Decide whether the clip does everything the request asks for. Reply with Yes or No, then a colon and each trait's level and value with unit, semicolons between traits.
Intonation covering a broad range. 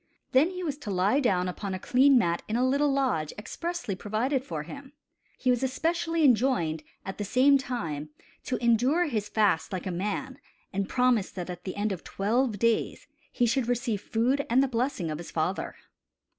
Yes: wide, 5.7 semitones